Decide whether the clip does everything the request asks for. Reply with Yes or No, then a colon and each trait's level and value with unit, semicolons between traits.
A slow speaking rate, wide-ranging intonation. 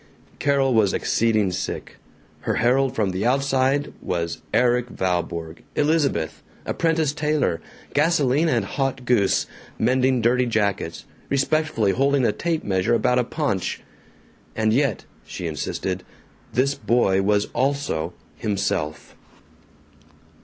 Yes: slow, 115 wpm; wide, 5.8 semitones